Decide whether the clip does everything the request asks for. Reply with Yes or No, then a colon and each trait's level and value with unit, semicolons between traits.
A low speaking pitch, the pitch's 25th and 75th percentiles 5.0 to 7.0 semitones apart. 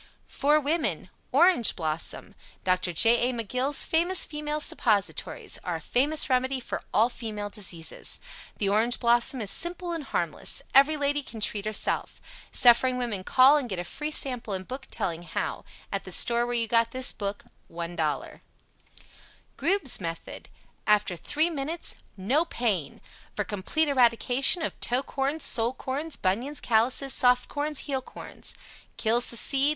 No: high, 245 Hz; average, 5.3 semitones